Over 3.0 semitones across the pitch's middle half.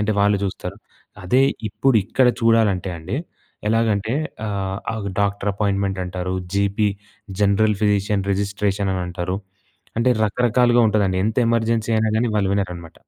No: narrow, 2.4 semitones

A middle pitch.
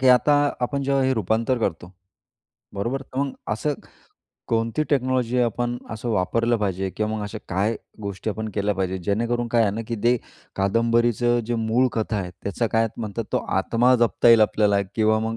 No: low, 115 Hz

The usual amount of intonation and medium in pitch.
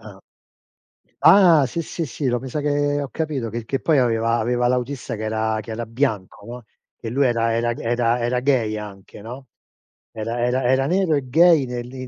No: average, 3.4 semitones; low, 125 Hz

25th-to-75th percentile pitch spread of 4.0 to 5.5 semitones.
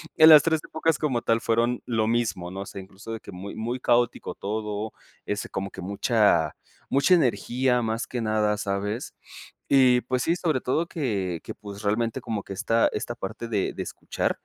No: average, 3.6 semitones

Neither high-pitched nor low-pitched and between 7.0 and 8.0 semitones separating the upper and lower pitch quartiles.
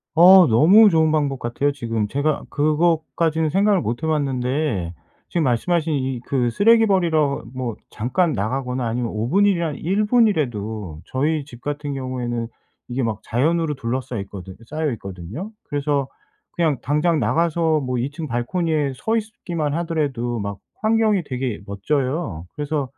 No: medium, 145 Hz; average, 5.3 semitones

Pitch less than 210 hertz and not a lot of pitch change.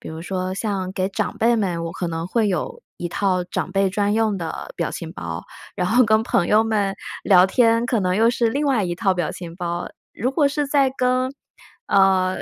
No: high, 200 Hz; average, 3.9 semitones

